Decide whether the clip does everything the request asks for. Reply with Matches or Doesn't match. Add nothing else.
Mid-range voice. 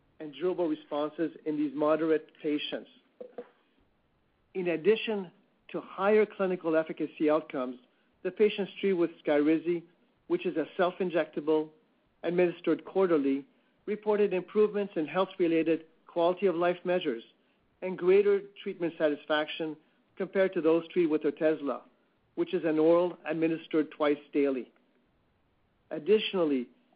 Matches